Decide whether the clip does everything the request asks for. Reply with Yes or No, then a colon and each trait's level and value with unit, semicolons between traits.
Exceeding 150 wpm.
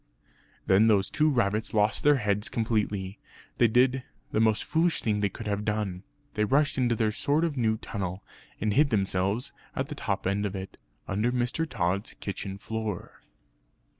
Yes: average, 170 wpm